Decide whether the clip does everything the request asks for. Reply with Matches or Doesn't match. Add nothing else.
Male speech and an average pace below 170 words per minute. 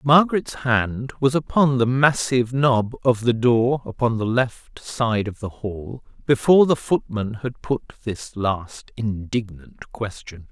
Matches